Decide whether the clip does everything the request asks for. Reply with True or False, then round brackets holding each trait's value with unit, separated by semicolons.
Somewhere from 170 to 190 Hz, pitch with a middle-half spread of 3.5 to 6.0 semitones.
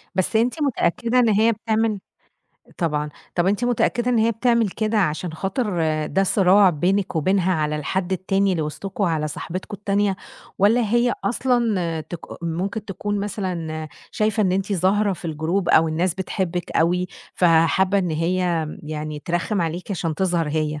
True (185 Hz; 3.9 semitones)